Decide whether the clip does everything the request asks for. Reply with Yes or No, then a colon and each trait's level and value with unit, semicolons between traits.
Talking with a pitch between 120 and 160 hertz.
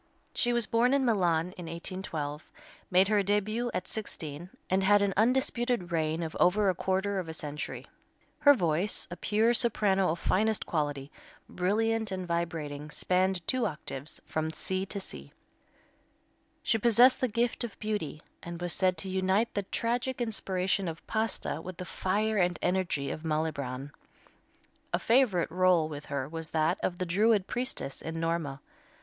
No: medium, 185 Hz